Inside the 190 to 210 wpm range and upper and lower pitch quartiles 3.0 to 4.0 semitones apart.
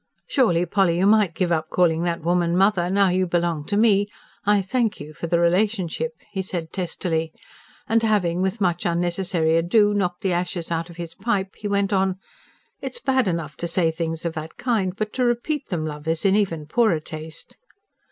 Yes: average, 195 wpm; average, 3.3 semitones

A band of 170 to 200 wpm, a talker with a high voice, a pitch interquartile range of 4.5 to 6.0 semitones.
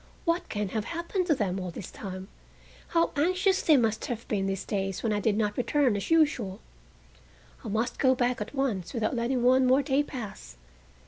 Yes: average, 195 wpm; high, 235 Hz; wide, 5.6 semitones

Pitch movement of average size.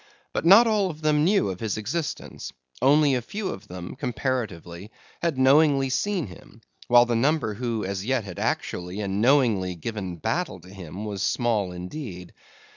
No: wide, 7.3 semitones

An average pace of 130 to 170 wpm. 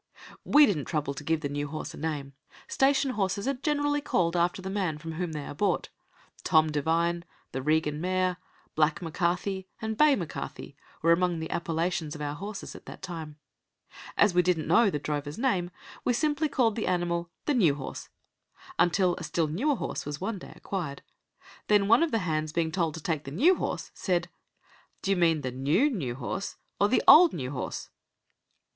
No: average, 190 wpm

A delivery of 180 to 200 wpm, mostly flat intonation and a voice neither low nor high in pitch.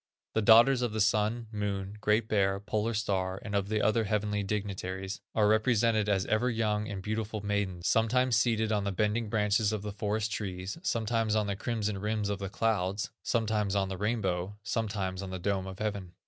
No: average, 190 wpm; narrow, 1.9 semitones; low, 105 Hz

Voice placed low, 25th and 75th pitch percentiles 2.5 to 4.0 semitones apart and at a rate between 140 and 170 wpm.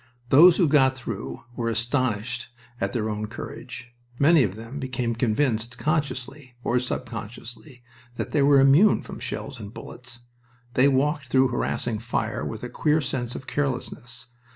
Yes: low, 125 Hz; average, 3.1 semitones; average, 155 wpm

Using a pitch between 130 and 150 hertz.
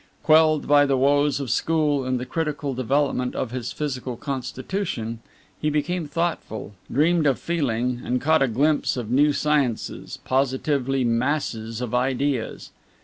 Yes: medium, 140 Hz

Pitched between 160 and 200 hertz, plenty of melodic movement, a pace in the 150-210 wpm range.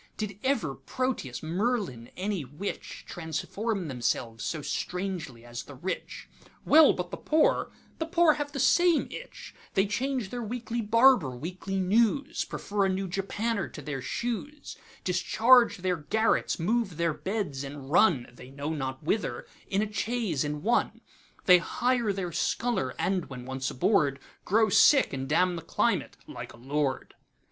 No: high, 190 Hz; wide, 7.9 semitones; slow, 135 wpm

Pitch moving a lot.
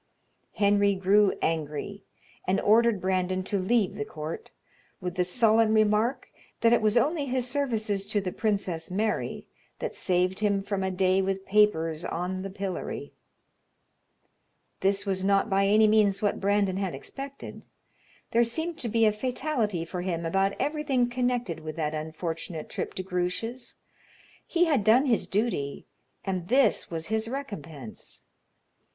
No: average, 3.7 semitones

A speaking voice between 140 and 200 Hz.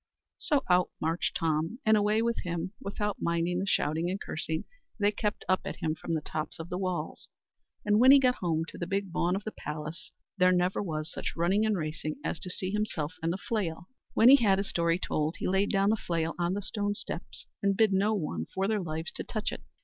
Yes: medium, 185 Hz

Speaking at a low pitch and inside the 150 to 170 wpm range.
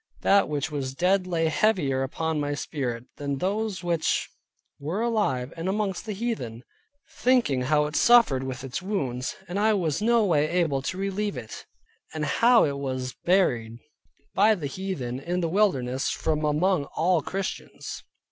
No: medium, 160 Hz; average, 160 wpm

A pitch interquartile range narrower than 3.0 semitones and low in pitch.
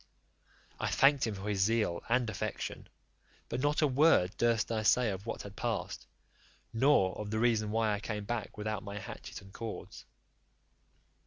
Yes: narrow, 2.5 semitones; low, 110 Hz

